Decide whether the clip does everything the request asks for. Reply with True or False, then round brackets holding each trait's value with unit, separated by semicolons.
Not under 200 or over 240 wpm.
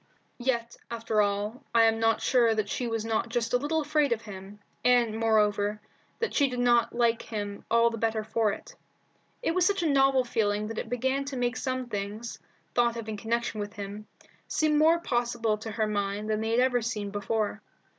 True (205 wpm)